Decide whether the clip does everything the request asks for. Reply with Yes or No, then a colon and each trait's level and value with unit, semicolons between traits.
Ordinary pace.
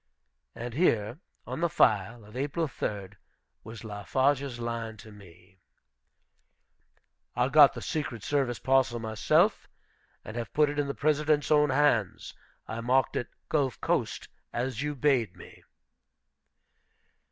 No: slow, 130 wpm